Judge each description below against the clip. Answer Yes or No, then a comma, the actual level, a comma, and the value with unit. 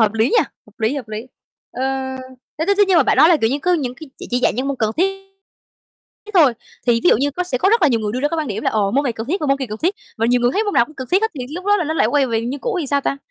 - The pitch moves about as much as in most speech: No, wide, 6.1 semitones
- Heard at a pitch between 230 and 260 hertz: No, very high, 275 Hz